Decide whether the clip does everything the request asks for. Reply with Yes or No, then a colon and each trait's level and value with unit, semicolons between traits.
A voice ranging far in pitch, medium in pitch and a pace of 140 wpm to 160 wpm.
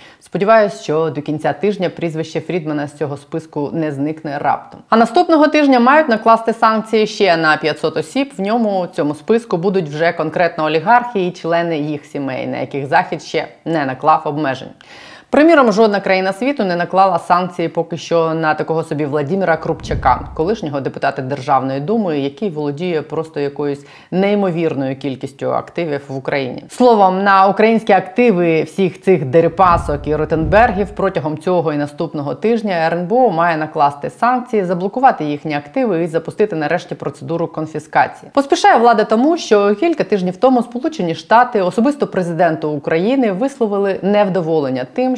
Yes: wide, 5.9 semitones; medium, 175 Hz; average, 145 wpm